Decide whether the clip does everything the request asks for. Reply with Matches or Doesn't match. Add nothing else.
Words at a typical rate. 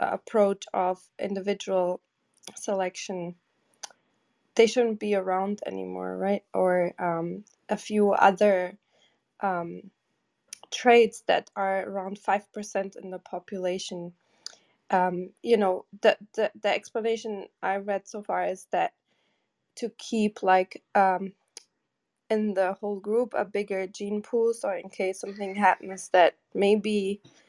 Doesn't match